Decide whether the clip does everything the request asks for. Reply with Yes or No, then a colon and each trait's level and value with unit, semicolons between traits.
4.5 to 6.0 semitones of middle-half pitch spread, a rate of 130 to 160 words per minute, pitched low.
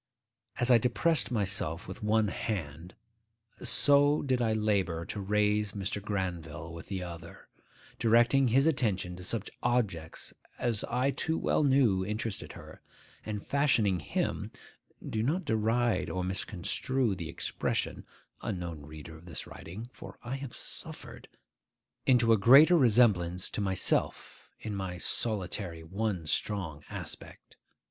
Yes: average, 5.0 semitones; slow, 135 wpm; low, 105 Hz